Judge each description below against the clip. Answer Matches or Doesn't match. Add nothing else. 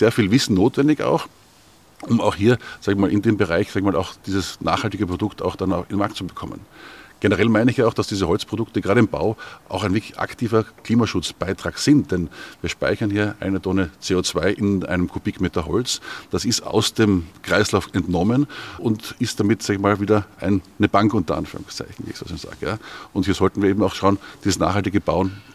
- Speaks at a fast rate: Matches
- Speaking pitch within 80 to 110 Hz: Matches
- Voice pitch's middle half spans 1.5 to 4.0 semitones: Matches